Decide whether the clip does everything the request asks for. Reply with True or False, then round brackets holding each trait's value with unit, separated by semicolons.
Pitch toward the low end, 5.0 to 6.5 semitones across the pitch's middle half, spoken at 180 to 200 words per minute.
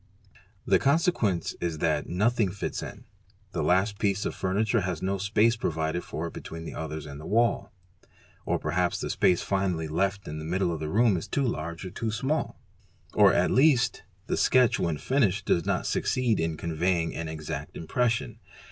True (95 Hz; 5.4 semitones; 190 wpm)